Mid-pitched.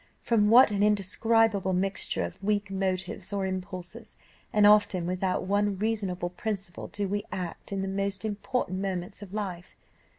No: high, 195 Hz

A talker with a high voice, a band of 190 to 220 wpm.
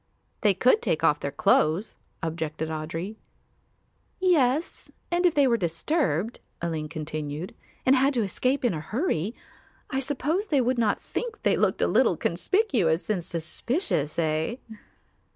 No: high, 215 Hz; average, 145 wpm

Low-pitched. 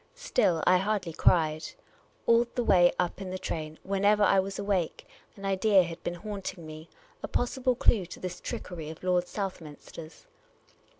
No: medium, 185 Hz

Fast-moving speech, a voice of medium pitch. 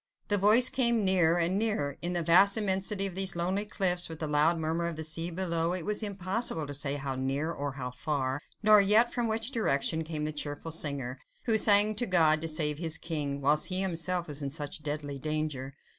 Yes: fast, 215 wpm; medium, 165 Hz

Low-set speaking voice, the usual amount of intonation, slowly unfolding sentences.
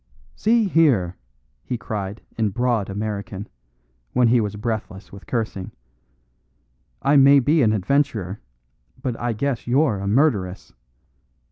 Yes: low, 115 Hz; average, 5.0 semitones; slow, 125 wpm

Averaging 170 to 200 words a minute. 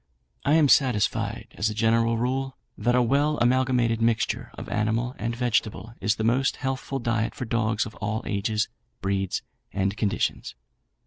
No: average, 155 wpm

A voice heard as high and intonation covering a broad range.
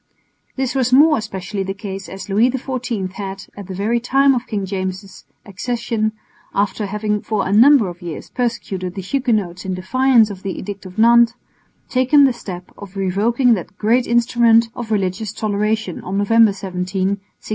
No: high, 210 Hz; average, 3.7 semitones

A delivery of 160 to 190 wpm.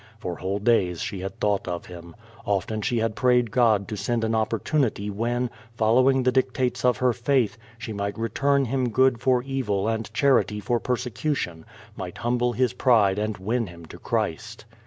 Yes: average, 180 wpm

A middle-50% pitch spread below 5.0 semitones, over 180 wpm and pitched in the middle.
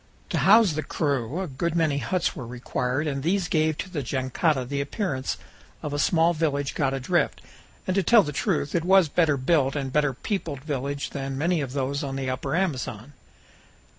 Yes: average, 3.8 semitones; average, 195 wpm; medium, 145 Hz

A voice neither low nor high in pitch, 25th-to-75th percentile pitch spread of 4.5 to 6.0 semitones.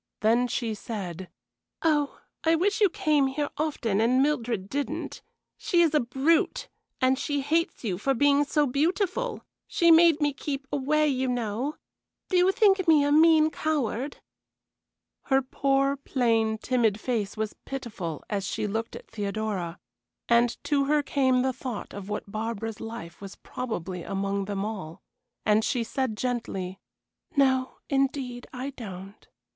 No: very high, 255 Hz; average, 5.1 semitones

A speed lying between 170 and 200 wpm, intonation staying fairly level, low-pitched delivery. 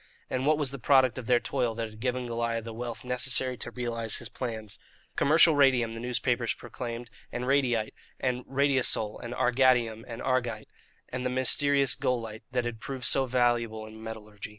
Yes: average, 175 wpm; narrow, 2.2 semitones; low, 120 Hz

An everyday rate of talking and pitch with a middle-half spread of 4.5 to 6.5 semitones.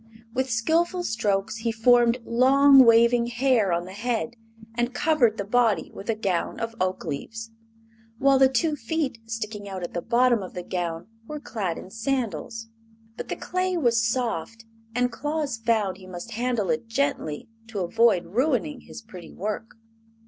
No: average, 165 wpm; average, 3.7 semitones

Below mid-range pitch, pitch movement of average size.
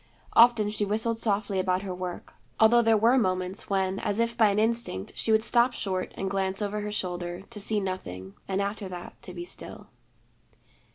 No: high, 200 Hz; average, 3.0 semitones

